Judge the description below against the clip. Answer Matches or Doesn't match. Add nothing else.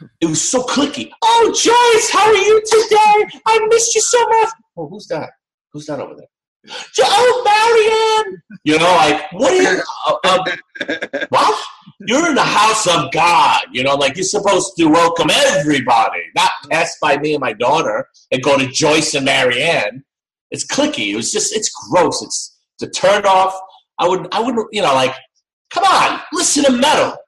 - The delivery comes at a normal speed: Matches